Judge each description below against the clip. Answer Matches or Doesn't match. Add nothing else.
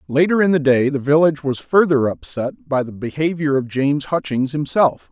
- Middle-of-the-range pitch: Matches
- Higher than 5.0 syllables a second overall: Matches